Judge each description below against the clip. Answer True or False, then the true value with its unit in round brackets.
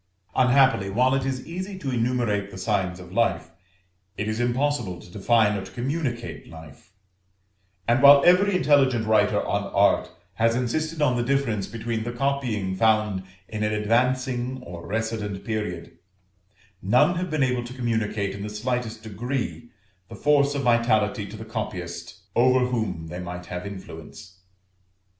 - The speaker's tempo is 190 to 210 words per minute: False (155 wpm)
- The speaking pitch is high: False (115 Hz)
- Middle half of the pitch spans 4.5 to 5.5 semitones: False (4.1 semitones)